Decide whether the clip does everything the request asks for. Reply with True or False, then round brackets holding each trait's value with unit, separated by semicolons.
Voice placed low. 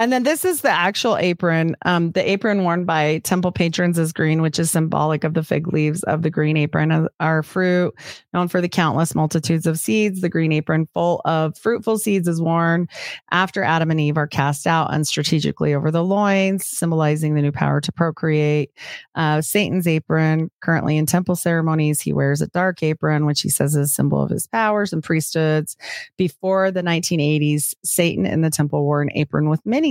False (165 Hz)